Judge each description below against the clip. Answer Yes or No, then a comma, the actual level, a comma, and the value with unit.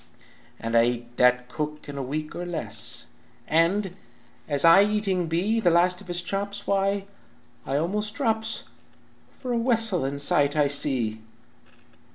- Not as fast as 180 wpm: Yes, average, 155 wpm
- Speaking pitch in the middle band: Yes, medium, 170 Hz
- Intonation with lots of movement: Yes, wide, 6.2 semitones